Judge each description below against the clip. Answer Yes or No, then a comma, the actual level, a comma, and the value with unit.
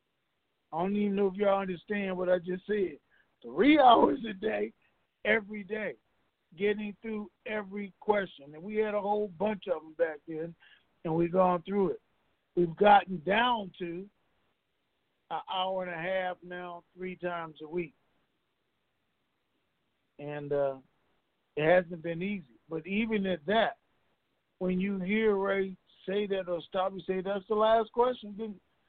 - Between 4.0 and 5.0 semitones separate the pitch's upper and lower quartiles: No, average, 2.9 semitones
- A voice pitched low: No, high, 190 Hz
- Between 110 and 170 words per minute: Yes, average, 155 wpm